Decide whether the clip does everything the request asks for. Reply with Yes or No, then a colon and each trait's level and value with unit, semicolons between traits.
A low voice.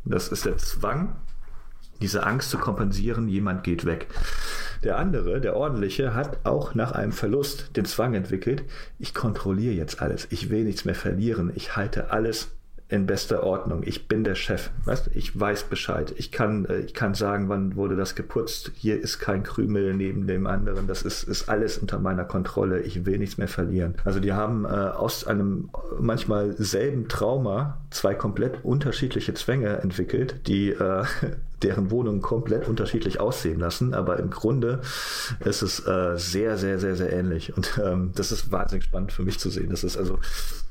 Yes: low, 100 Hz